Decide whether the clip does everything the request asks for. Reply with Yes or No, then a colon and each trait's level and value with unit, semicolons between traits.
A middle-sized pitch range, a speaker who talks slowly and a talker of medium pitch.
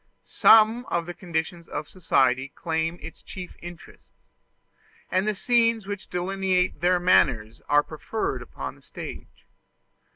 Yes: average, 3.3 semitones; slow, 130 wpm; medium, 175 Hz